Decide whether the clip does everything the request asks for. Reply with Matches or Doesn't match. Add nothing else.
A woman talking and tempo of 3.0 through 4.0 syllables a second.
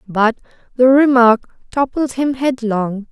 Matches